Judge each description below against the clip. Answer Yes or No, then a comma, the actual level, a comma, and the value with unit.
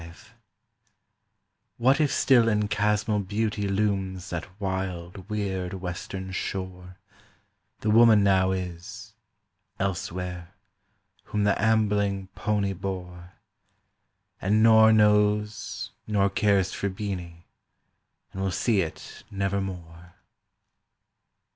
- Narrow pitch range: Yes, narrow, 2.2 semitones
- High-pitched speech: No, low, 100 Hz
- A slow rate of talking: Yes, slow, 90 wpm